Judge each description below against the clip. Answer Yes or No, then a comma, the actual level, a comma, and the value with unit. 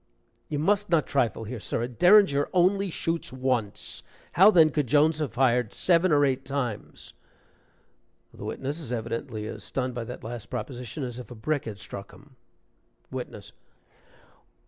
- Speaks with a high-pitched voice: No, low, 135 Hz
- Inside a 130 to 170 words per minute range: Yes, average, 160 wpm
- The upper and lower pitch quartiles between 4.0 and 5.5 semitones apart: Yes, average, 4.9 semitones